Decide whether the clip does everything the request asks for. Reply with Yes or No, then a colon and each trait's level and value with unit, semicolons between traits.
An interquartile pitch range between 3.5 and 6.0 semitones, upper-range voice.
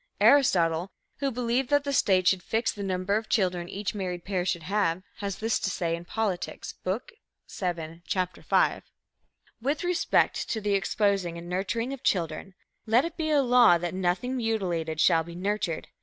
Yes: average, 4.6 semitones; high, 195 Hz